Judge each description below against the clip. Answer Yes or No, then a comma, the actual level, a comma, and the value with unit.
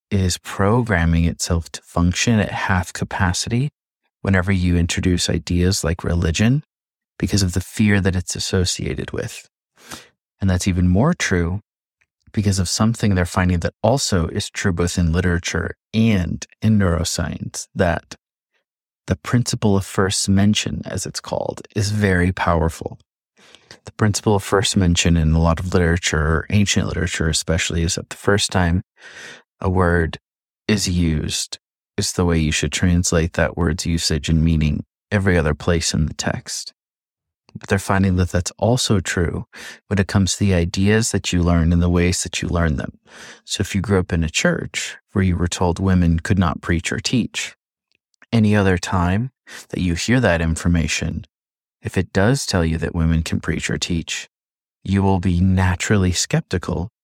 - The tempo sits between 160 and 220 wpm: Yes, average, 165 wpm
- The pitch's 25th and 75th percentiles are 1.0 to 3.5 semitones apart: Yes, average, 3.2 semitones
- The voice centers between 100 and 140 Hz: No, very low, 90 Hz